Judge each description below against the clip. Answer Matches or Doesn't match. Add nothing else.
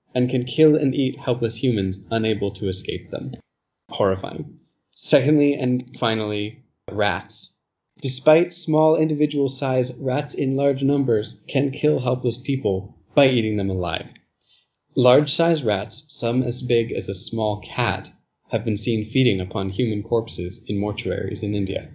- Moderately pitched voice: Doesn't match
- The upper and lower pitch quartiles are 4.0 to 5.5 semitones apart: Matches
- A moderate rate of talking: Matches